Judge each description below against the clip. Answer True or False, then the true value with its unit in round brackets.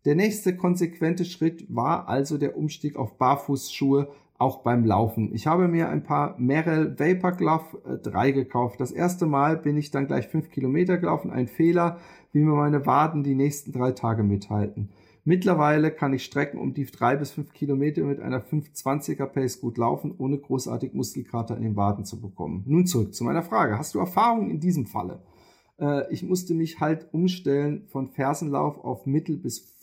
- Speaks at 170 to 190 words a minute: True (185 wpm)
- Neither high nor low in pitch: True (145 Hz)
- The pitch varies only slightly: False (4.1 semitones)